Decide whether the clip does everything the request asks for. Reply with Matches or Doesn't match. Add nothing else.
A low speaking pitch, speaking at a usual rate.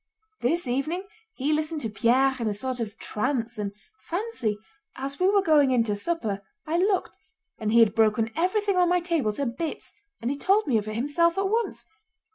Doesn't match